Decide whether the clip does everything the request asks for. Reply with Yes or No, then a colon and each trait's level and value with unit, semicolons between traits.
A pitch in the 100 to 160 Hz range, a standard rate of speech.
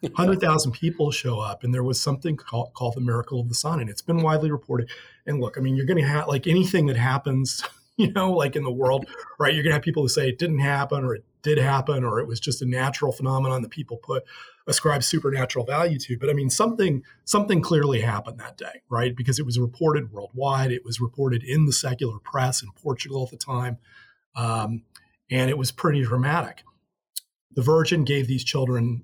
No: low, 135 Hz; fast, 215 wpm